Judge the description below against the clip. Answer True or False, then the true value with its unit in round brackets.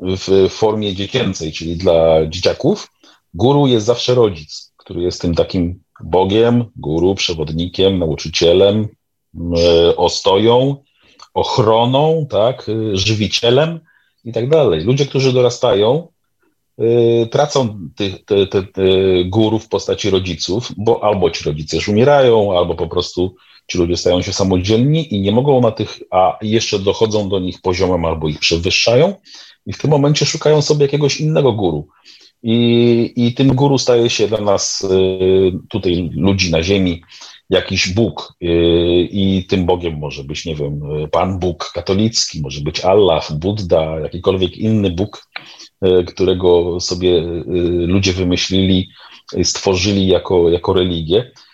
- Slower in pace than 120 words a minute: False (130 wpm)